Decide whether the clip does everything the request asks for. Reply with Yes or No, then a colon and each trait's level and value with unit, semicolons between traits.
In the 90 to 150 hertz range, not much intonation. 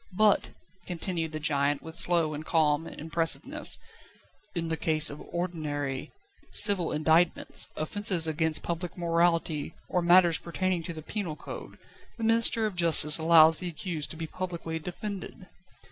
No: medium, 165 Hz; narrow, 2.2 semitones